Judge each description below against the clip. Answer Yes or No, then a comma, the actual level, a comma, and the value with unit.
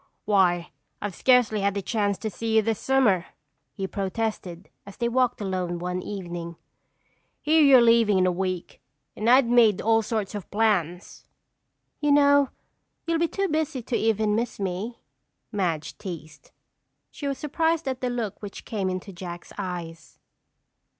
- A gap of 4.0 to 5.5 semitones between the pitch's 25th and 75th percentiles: Yes, average, 4.8 semitones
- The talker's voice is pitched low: No, high, 210 Hz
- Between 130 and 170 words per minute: Yes, average, 155 wpm